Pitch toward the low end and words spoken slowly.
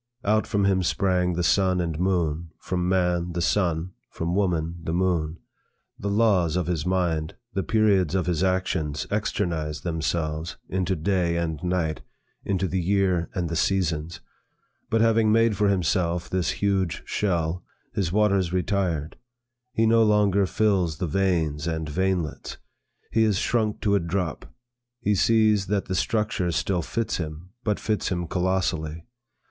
No: very low, 90 Hz; average, 155 wpm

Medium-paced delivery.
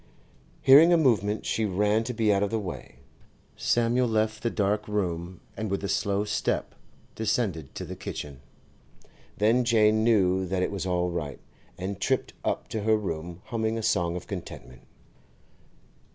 Yes: average, 160 wpm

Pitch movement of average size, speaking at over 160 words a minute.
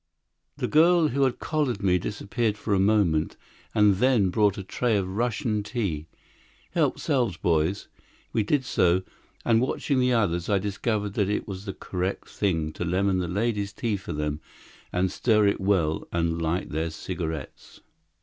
Yes: average, 4.2 semitones; average, 170 wpm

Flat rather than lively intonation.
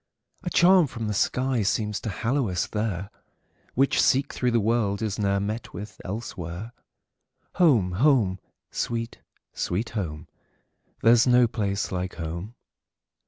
No: average, 3.9 semitones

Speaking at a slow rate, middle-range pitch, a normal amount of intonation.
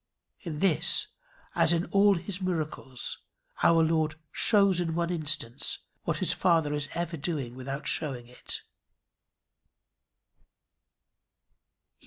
Yes: slow, 110 wpm; medium, 160 Hz; average, 3.0 semitones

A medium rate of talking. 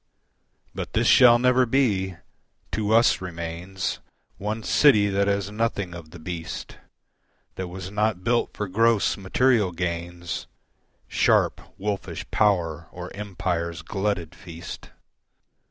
No: slow, 120 wpm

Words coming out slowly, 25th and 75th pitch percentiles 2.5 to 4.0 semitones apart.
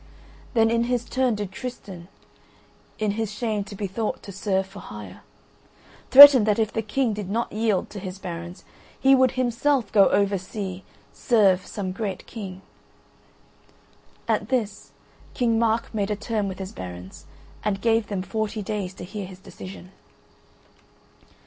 No: average, 155 wpm; average, 3.1 semitones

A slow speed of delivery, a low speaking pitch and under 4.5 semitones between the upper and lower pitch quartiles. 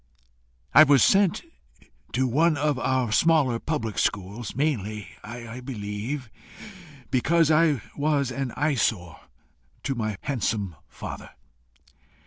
No: slow, 110 wpm; low, 130 Hz; average, 5.2 semitones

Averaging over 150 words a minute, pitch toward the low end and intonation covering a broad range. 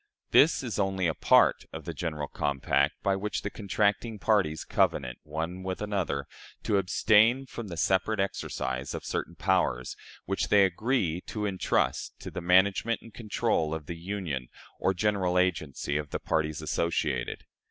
No: average, 160 wpm; very low, 95 Hz; average, 4.6 semitones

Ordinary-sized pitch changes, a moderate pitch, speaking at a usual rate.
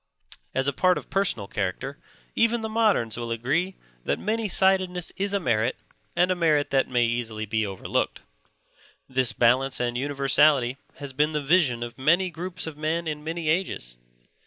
No: wide, 6.7 semitones; medium, 145 Hz; average, 170 wpm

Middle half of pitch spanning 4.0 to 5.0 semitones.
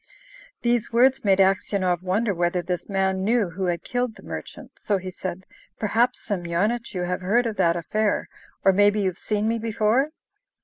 No: average, 3.5 semitones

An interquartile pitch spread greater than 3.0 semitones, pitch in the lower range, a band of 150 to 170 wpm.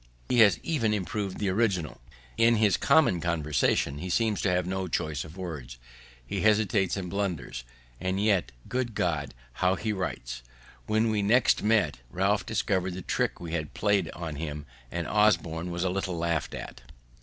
Yes: average, 4.2 semitones; very low, 95 Hz; average, 165 wpm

